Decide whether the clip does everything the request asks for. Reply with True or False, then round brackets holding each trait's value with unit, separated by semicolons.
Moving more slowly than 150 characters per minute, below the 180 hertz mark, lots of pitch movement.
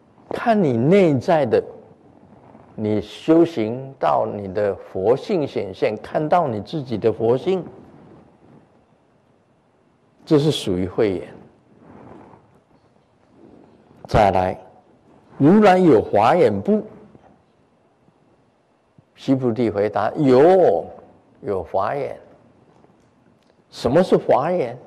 True (125 characters per minute; 135 Hz; 8.6 semitones)